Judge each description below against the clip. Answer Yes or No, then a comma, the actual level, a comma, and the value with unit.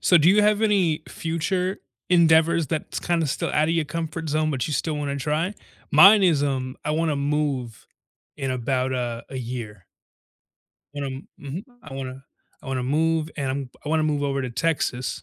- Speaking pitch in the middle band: Yes, medium, 150 Hz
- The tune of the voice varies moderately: Yes, average, 3.6 semitones